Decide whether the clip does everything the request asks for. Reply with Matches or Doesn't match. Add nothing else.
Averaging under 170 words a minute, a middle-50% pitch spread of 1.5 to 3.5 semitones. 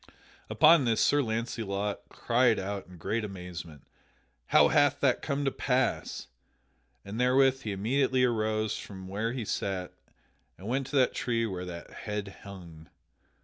Doesn't match